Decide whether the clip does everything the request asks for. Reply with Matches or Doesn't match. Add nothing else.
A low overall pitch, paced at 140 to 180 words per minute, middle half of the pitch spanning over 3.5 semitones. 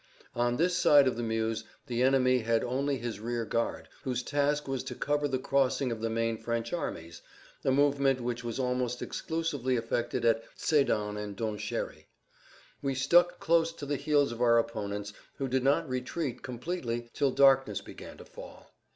Doesn't match